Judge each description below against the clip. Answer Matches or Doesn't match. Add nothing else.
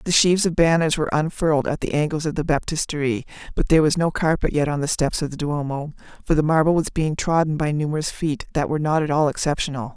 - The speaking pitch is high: Doesn't match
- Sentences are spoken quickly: Matches